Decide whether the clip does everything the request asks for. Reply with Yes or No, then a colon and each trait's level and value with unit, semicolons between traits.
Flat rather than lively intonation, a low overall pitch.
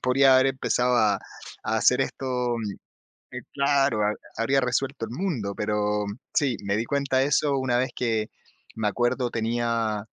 No: average, 3.6 semitones; low, 125 Hz